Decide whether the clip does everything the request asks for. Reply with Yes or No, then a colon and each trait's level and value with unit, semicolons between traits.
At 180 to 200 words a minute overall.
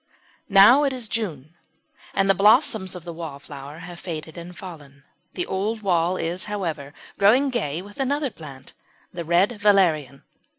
No: average, 160 wpm